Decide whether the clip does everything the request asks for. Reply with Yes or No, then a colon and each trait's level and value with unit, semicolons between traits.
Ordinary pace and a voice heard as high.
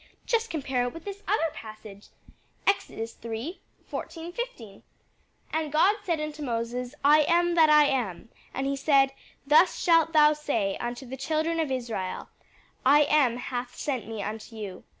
Yes: average, 160 wpm; very high, 275 Hz